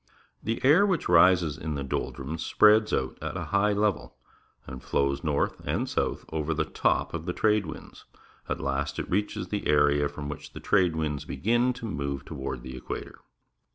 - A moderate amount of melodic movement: No, wide, 6.2 semitones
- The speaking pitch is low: Yes, very low, 80 Hz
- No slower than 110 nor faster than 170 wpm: No, average, 185 wpm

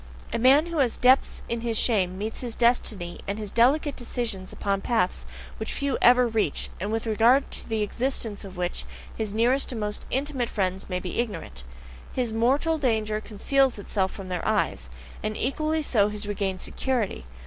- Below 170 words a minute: No, average, 180 wpm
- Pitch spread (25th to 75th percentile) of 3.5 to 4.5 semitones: Yes, average, 4.0 semitones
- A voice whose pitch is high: Yes, high, 225 Hz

